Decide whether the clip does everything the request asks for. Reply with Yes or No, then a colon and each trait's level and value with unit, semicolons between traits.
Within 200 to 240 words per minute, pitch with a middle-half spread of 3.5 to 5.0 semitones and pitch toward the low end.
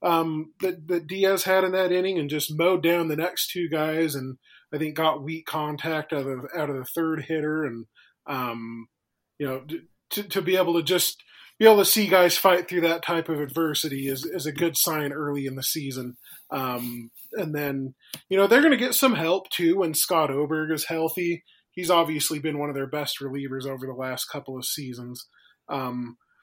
No: fast, 205 wpm; average, 4.2 semitones; medium, 155 Hz